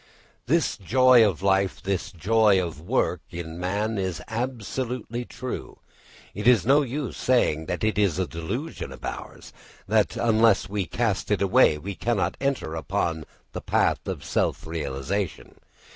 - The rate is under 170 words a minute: Yes, average, 155 wpm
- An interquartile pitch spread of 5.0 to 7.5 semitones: Yes, wide, 5.5 semitones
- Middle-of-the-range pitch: No, low, 100 Hz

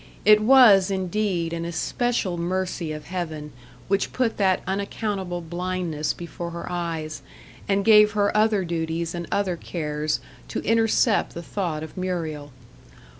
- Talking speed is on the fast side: No, slow, 135 wpm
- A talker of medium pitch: Yes, medium, 180 Hz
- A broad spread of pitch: No, average, 3.4 semitones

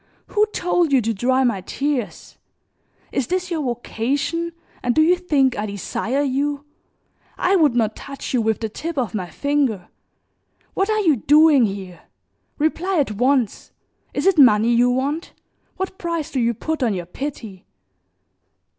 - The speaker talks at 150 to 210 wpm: Yes, average, 160 wpm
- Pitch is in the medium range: No, very high, 270 Hz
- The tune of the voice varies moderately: No, wide, 5.9 semitones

